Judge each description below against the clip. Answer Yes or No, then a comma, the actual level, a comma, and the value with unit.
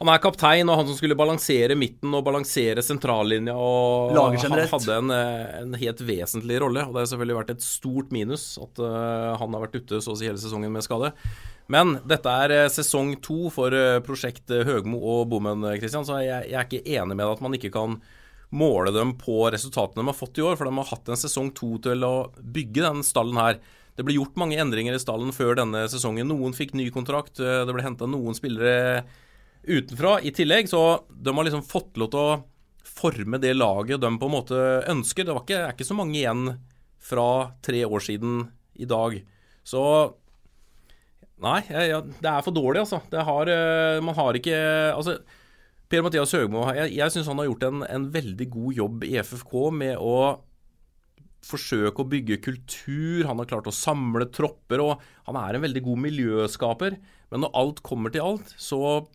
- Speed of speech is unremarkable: Yes, average, 195 wpm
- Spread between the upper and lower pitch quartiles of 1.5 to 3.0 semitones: No, average, 4.0 semitones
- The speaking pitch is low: Yes, low, 130 Hz